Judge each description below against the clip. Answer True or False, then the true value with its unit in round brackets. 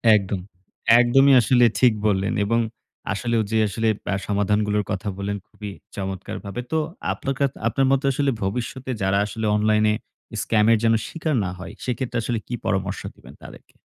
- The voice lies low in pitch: True (110 Hz)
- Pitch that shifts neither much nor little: True (3.4 semitones)